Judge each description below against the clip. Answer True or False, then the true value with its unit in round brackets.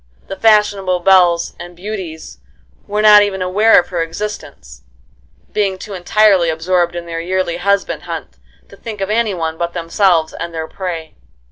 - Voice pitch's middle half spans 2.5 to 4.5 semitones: True (3.2 semitones)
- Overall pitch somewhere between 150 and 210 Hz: True (185 Hz)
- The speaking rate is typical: True (160 wpm)